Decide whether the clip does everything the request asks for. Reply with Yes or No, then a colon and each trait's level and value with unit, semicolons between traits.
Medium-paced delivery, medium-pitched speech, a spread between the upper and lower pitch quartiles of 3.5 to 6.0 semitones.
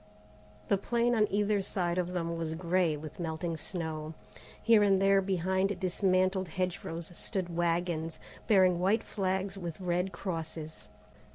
No: average, 145 wpm; medium, 180 Hz; narrow, 2.6 semitones